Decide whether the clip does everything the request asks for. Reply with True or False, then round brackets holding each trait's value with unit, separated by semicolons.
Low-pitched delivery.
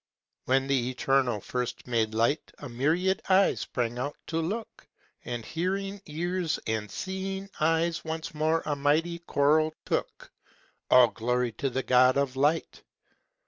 False (145 Hz)